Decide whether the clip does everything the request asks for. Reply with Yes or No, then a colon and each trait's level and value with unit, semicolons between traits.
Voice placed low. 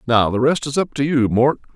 Yes: low, 130 Hz